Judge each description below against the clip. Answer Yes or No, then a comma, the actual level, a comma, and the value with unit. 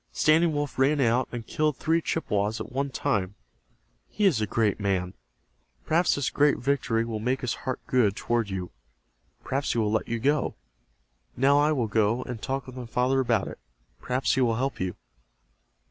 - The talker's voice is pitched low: Yes, low, 125 Hz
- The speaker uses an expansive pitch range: No, average, 4.1 semitones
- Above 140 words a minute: Yes, average, 185 wpm